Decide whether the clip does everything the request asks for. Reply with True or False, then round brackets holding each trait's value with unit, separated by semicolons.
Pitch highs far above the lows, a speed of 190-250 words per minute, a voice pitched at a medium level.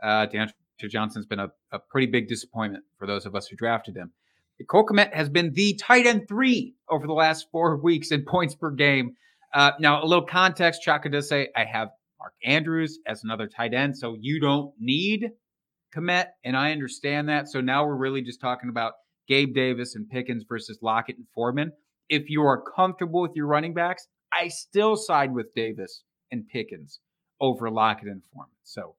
True (6.3 semitones; 195 wpm; 145 Hz)